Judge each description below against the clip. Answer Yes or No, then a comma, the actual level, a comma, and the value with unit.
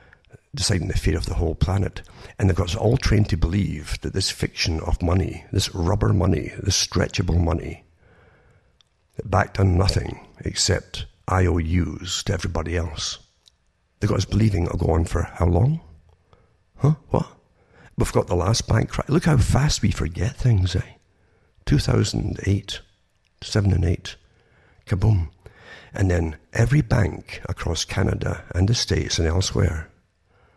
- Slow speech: No, average, 145 wpm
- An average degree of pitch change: Yes, average, 3.6 semitones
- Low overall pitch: Yes, very low, 95 Hz